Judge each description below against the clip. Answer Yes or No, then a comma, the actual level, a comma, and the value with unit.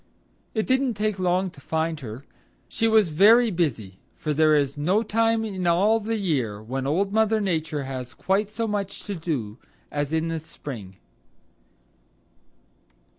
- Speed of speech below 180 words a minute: Yes, average, 155 wpm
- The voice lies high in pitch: No, medium, 170 Hz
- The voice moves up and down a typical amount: No, wide, 6.7 semitones